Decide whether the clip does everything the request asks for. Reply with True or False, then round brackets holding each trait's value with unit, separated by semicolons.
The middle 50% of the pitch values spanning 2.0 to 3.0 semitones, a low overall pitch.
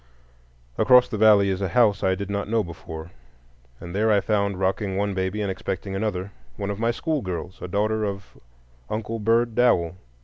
True (2.6 semitones; 100 Hz)